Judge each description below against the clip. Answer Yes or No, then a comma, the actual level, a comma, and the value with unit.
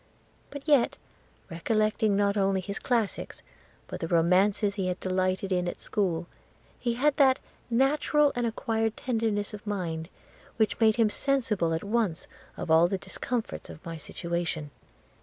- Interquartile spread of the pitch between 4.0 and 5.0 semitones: Yes, average, 4.5 semitones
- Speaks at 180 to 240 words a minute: No, average, 150 wpm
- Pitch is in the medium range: No, high, 205 Hz